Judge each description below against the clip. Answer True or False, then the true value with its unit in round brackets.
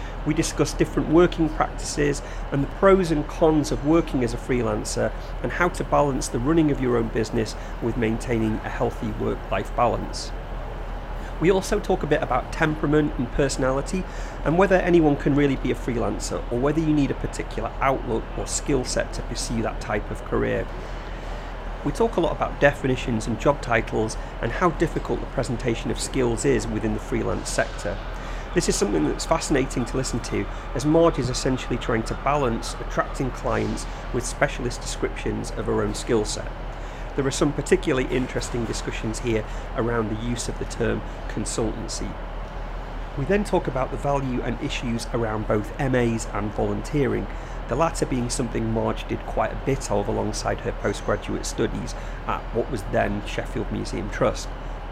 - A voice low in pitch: True (125 Hz)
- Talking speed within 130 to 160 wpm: False (175 wpm)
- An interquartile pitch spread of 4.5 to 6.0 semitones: True (4.8 semitones)